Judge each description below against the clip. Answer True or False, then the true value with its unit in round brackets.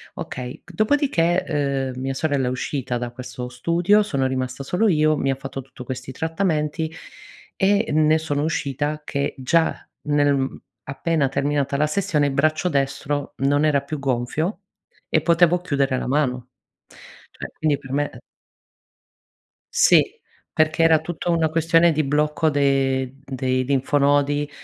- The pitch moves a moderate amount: True (3.0 semitones)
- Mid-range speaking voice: True (145 Hz)